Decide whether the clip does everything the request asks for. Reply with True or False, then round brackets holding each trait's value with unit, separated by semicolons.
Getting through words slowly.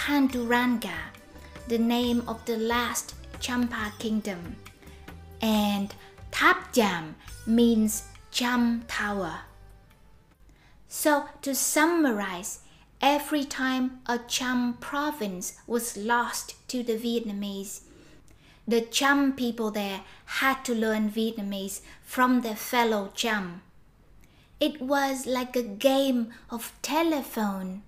True (100 wpm)